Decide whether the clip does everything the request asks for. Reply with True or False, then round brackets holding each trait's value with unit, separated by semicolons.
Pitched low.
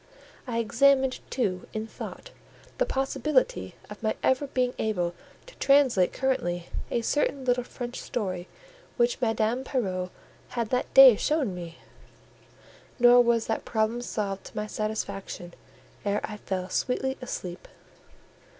False (235 Hz)